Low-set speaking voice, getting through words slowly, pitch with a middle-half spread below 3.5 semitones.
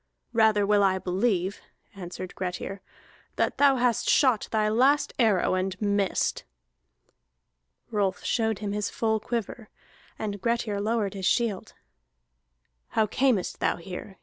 No: high, 210 Hz; slow, 125 wpm; average, 2.9 semitones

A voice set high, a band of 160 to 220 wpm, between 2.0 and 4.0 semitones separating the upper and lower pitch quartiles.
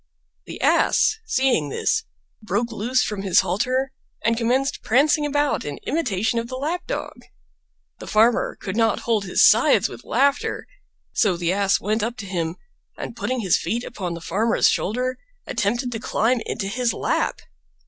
No: high, 230 Hz; average, 165 wpm; average, 4.4 semitones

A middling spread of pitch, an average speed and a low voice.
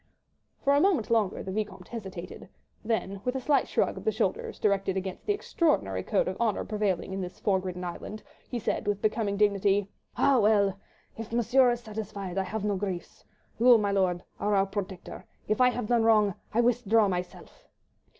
No: average, 3.3 semitones; average, 185 wpm; high, 205 Hz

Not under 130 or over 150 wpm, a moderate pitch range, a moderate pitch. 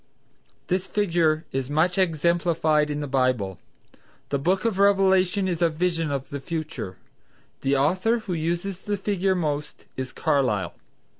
Yes: average, 145 wpm; average, 4.6 semitones; medium, 165 Hz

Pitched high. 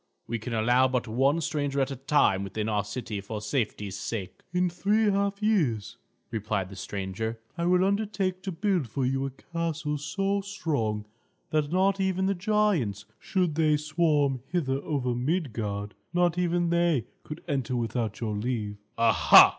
No: medium, 140 Hz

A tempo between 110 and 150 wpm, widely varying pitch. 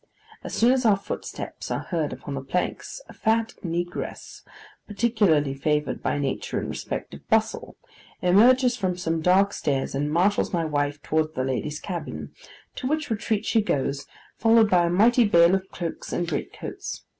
No: average, 170 wpm; wide, 6.5 semitones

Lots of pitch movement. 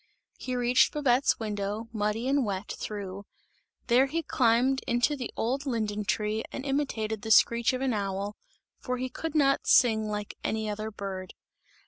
No: average, 3.7 semitones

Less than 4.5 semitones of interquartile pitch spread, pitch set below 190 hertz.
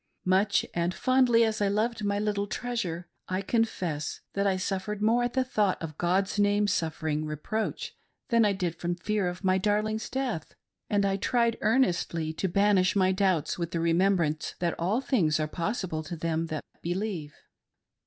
No: average, 4.0 semitones; high, 195 Hz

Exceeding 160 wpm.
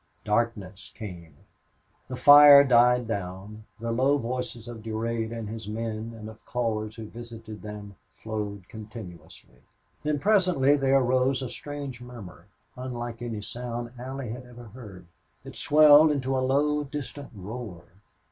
No: average, 140 wpm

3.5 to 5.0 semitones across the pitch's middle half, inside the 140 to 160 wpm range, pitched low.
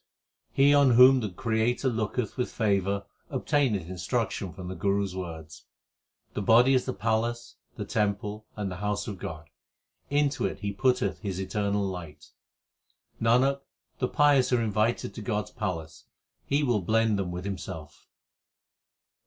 Yes: average, 4.4 semitones; average, 155 wpm; low, 105 Hz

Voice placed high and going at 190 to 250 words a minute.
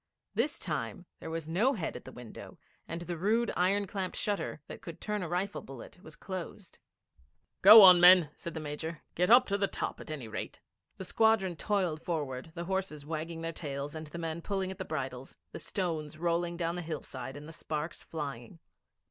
No: medium, 170 Hz; average, 200 wpm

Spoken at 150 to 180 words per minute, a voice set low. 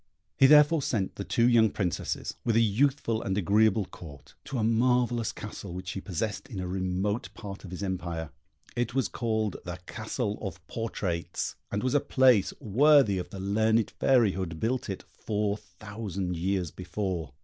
Yes: average, 175 wpm; low, 105 Hz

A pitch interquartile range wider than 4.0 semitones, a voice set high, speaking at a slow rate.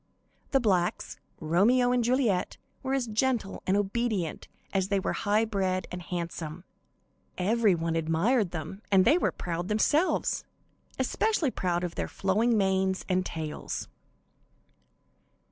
Yes: average, 4.8 semitones; high, 195 Hz; slow, 130 wpm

